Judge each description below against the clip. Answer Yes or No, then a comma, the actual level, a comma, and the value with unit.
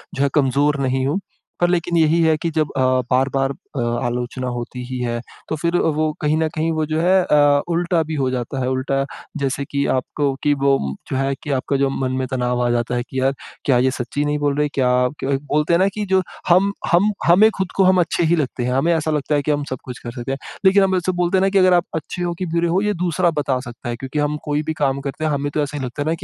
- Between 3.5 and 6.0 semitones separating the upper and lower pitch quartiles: Yes, average, 4.3 semitones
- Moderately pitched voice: Yes, medium, 145 Hz